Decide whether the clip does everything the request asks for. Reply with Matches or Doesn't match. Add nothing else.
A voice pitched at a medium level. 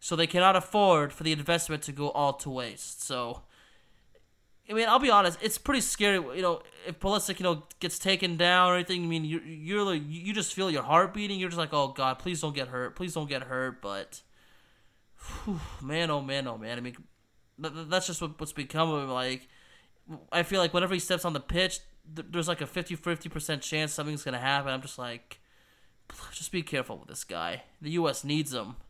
Matches